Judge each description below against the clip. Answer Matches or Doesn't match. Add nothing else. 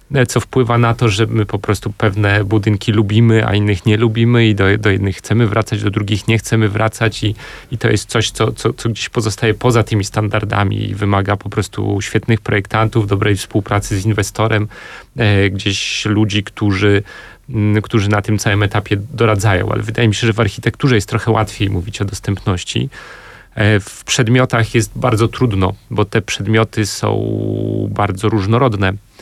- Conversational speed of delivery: Doesn't match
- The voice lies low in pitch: Matches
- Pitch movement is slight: Matches